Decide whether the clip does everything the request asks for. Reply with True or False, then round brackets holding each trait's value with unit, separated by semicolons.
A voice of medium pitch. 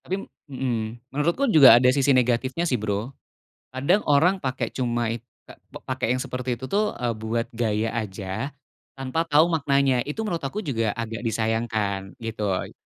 False (125 Hz)